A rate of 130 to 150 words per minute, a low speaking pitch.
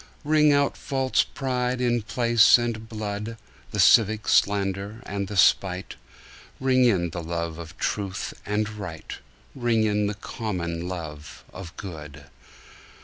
Yes: slow, 135 wpm; low, 105 Hz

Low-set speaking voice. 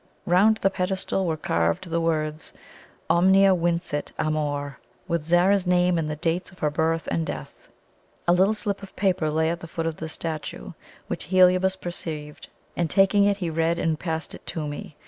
No: medium, 170 Hz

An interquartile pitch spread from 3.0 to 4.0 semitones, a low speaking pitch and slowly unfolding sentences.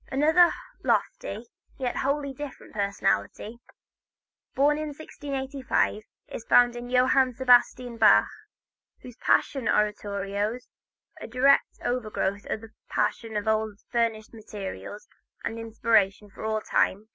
No: average, 3.7 semitones; high, 230 Hz; slow, 120 wpm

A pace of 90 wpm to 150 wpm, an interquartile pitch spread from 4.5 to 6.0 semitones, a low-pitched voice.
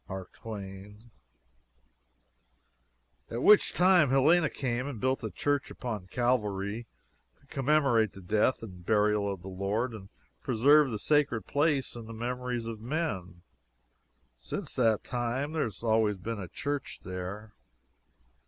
Yes: slow, 135 wpm; average, 4.8 semitones; low, 115 Hz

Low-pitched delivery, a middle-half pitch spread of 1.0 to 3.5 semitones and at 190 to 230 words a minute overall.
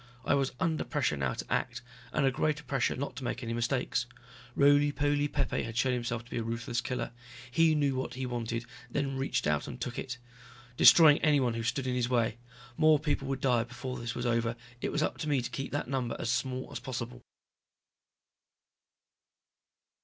Yes: low, 125 Hz; average, 3.0 semitones; average, 200 wpm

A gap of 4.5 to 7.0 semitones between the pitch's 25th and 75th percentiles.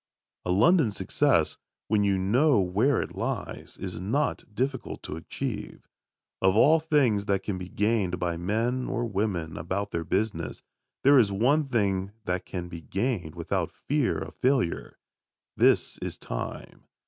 Yes: wide, 5.6 semitones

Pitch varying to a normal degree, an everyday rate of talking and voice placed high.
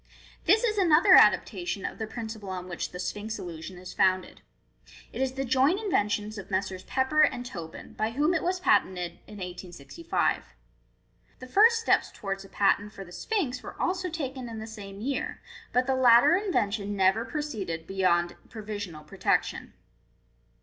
No: wide, 7.5 semitones; average, 170 wpm; high, 220 Hz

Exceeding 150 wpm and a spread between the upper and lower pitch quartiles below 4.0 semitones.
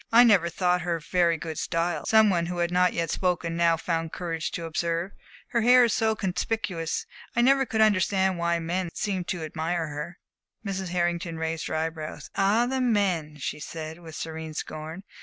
Yes: average, 190 wpm; average, 3.1 semitones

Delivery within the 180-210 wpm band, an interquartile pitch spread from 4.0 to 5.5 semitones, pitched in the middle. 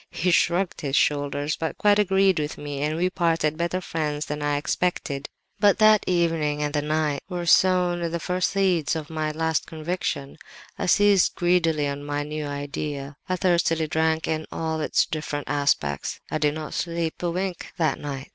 No: average, 185 wpm; average, 3.0 semitones; medium, 160 Hz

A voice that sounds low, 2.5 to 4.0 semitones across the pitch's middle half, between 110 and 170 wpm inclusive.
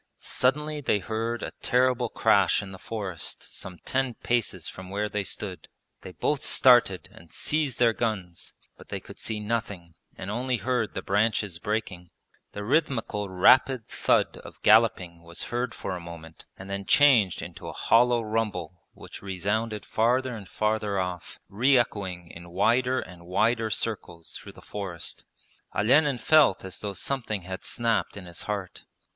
No: low, 105 Hz; average, 4.5 semitones; average, 160 wpm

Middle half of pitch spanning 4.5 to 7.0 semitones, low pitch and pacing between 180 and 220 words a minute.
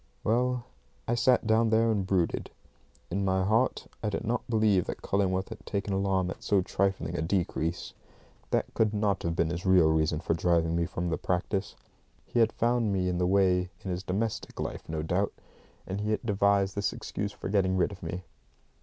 No: average, 3.0 semitones; very low, 95 Hz; average, 200 wpm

